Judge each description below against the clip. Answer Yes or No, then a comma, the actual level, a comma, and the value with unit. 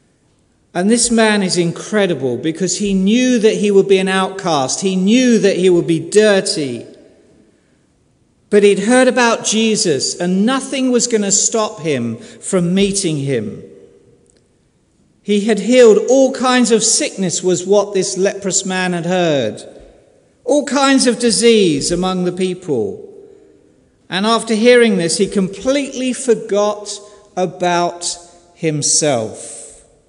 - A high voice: Yes, high, 200 Hz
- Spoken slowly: Yes, slow, 130 wpm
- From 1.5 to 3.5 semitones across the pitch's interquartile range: No, average, 4.4 semitones